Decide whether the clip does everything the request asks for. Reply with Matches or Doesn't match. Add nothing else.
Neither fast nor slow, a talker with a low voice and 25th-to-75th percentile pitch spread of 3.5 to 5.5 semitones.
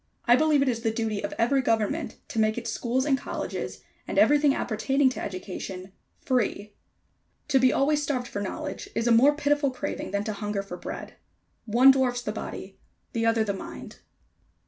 Doesn't match